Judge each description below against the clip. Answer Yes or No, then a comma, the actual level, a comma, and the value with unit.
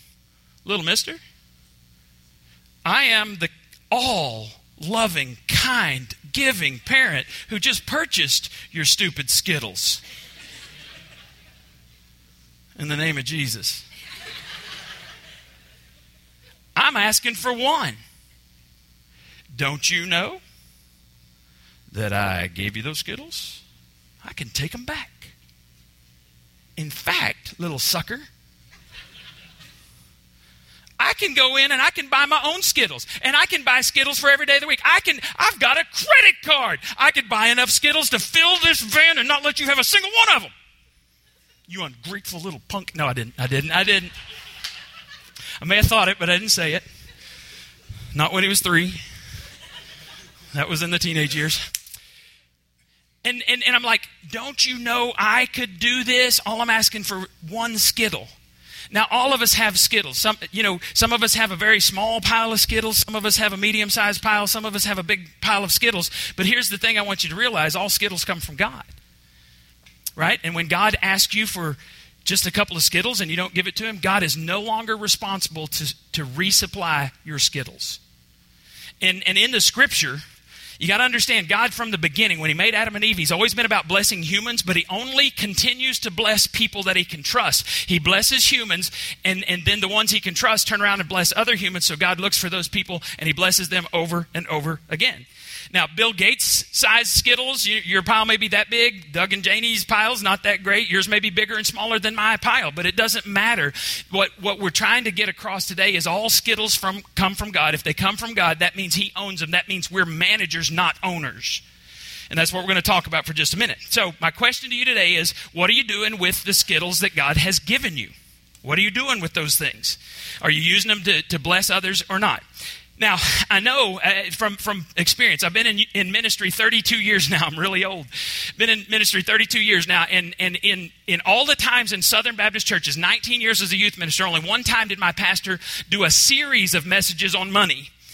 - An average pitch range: No, wide, 6.1 semitones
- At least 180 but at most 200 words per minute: Yes, average, 195 wpm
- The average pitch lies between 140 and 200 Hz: Yes, high, 190 Hz